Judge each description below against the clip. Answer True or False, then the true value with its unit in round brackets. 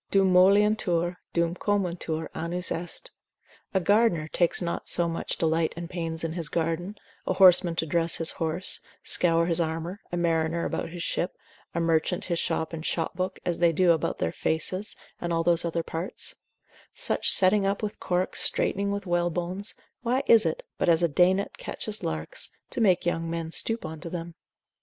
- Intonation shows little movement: True (2.0 semitones)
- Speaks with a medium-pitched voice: True (170 Hz)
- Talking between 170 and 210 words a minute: True (180 wpm)